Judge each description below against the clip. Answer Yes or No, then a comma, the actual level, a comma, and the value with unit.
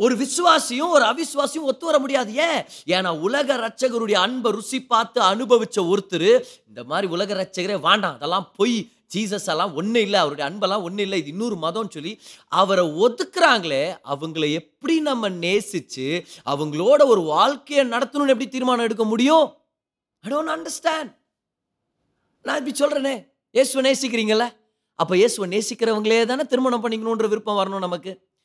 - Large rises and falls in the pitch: Yes, wide, 6.3 semitones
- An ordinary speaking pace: No, fast, 135 wpm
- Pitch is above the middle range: Yes, high, 230 Hz